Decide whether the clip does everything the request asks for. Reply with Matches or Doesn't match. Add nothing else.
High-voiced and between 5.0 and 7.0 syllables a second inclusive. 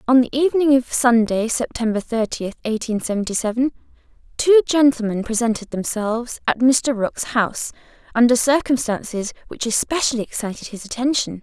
Matches